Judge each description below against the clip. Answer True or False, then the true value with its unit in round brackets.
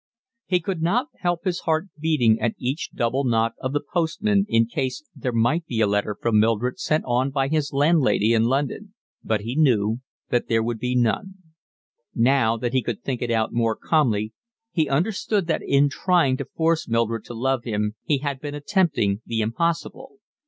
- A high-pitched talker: False (130 Hz)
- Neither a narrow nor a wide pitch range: False (5.7 semitones)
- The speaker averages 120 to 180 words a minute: False (190 wpm)